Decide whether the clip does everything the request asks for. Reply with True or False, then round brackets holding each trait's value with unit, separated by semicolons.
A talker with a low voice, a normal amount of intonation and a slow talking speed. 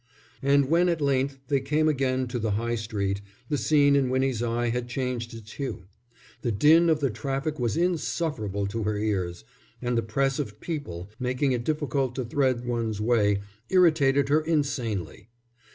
False (130 Hz; 4.1 semitones; 170 wpm)